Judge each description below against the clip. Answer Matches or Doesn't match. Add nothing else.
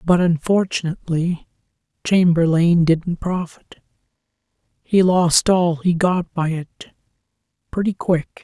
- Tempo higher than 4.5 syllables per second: Doesn't match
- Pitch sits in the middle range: Matches